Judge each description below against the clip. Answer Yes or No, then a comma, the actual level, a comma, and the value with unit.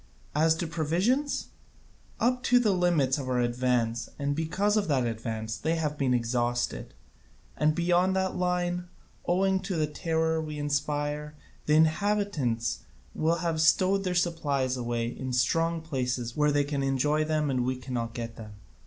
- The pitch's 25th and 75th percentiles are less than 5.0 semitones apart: No, average, 5.3 semitones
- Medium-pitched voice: Yes, medium, 150 Hz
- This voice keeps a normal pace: Yes, average, 160 wpm